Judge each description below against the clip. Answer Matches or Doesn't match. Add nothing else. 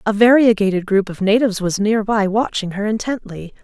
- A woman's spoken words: Matches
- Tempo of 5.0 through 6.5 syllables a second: Matches